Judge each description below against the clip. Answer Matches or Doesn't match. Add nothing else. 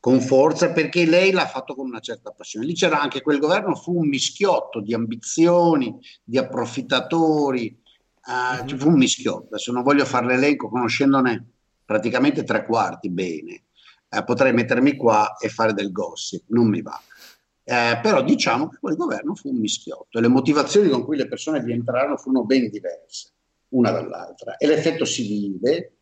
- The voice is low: Matches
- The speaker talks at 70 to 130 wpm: Doesn't match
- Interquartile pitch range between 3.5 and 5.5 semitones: Matches